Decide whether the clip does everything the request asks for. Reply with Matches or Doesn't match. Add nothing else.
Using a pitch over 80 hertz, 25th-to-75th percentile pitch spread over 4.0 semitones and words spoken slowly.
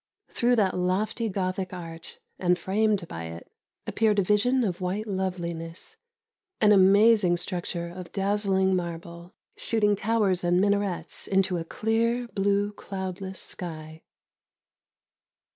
Doesn't match